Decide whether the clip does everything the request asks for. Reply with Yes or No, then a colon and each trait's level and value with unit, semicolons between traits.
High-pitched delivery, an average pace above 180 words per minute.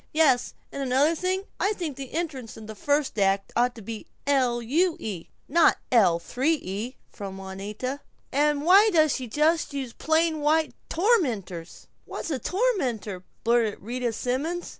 No: very high, 265 Hz; average, 160 wpm